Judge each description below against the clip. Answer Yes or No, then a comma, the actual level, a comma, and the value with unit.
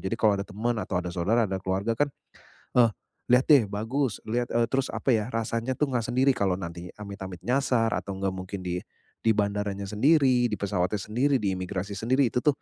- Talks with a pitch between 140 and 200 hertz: No, low, 110 Hz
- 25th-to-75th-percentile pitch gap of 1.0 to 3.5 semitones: No, average, 4.1 semitones